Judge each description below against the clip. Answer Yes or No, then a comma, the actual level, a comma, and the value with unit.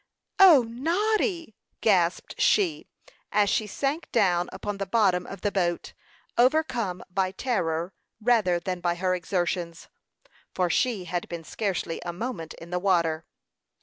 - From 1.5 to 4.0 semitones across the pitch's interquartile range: No, average, 5.3 semitones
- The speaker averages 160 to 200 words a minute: No, average, 140 wpm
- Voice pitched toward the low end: No, high, 190 Hz